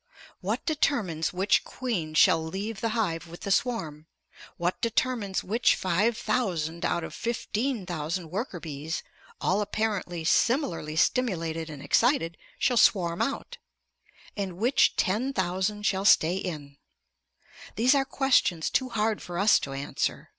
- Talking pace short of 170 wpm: Yes, average, 140 wpm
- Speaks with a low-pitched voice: No, high, 190 Hz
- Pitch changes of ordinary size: No, wide, 5.8 semitones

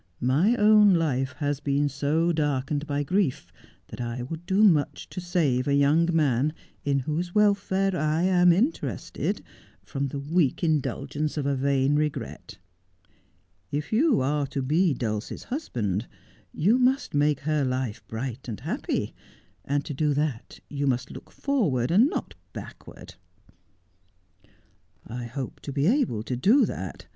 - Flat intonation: No, average, 4.8 semitones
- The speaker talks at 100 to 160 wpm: Yes, average, 150 wpm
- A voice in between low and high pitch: Yes, medium, 145 Hz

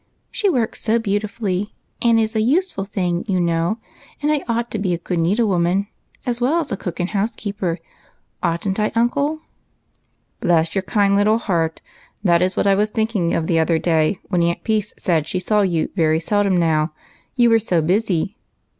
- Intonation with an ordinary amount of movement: Yes, average, 4.3 semitones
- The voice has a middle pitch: No, high, 195 Hz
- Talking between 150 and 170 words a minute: No, average, 185 wpm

